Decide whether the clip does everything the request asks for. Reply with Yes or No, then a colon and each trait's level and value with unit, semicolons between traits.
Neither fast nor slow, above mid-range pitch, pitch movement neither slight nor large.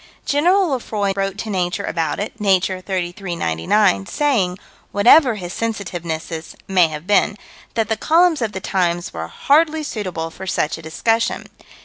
Yes: average, 150 wpm; high, 195 Hz; average, 4.6 semitones